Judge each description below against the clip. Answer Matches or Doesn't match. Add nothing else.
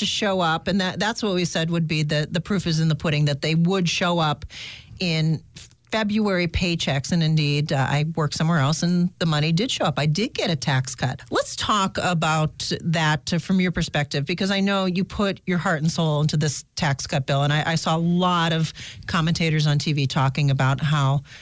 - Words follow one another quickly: Matches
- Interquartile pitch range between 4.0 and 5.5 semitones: Doesn't match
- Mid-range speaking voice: Matches